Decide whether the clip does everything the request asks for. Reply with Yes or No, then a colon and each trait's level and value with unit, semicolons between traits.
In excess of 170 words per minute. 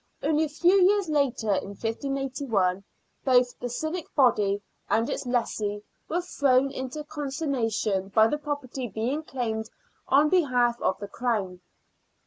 No: average, 140 wpm